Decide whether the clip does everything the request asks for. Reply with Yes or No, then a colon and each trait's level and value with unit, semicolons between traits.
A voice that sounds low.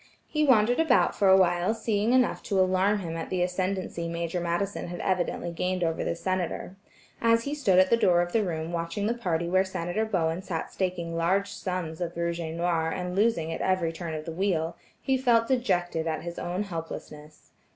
No: medium, 180 Hz